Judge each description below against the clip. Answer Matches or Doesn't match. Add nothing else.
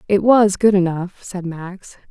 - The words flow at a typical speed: Matches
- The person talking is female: Matches